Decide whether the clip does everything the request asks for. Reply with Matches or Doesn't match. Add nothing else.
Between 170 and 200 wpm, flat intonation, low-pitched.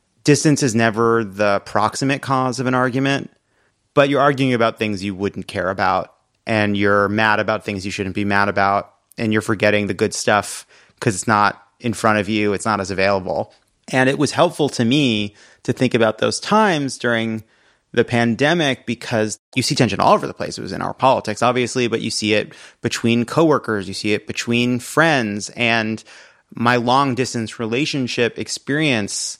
Doesn't match